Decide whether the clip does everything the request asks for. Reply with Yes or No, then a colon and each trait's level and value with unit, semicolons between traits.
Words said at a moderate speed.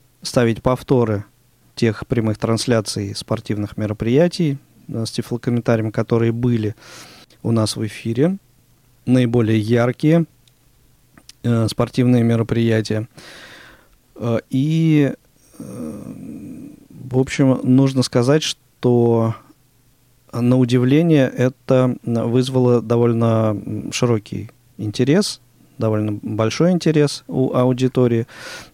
No: slow, 85 wpm